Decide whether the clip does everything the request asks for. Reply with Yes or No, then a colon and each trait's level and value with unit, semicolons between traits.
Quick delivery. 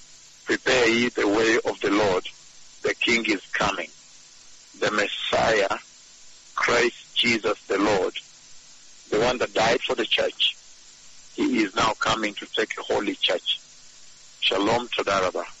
No: average, 140 wpm